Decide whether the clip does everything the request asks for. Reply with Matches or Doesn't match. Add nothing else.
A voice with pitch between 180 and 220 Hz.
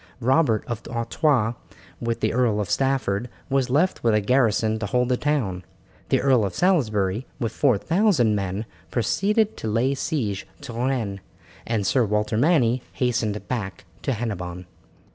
Doesn't match